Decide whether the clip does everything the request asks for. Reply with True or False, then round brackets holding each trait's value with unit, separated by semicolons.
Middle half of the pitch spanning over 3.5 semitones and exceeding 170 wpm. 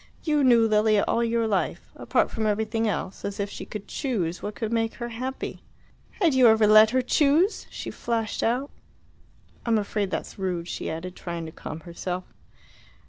False (3.2 semitones; 180 wpm)